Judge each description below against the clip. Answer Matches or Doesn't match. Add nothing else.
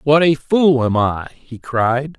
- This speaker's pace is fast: Doesn't match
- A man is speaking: Matches